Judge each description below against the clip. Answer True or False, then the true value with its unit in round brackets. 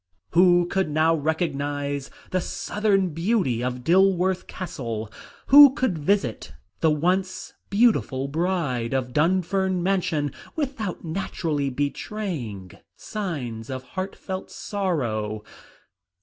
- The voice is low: False (170 Hz)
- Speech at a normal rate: False (100 wpm)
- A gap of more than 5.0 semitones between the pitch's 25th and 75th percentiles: True (5.5 semitones)